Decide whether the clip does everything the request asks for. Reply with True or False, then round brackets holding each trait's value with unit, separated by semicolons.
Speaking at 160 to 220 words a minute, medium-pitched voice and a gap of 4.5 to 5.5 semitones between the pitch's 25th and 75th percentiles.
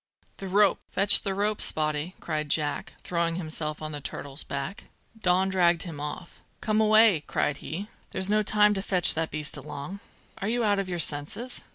True (185 wpm; 180 Hz; 4.8 semitones)